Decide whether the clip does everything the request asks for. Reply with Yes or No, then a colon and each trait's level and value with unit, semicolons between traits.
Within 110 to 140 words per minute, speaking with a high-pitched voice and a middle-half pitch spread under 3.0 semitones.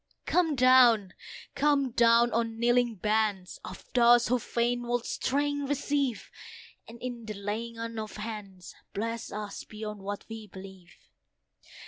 Yes: slow, 135 wpm; high, 230 Hz; narrow, 2.5 semitones